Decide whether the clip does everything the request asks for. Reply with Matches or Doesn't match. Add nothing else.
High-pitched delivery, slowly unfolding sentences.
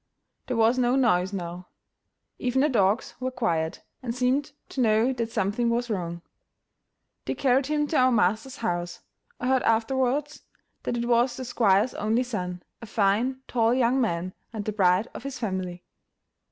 Doesn't match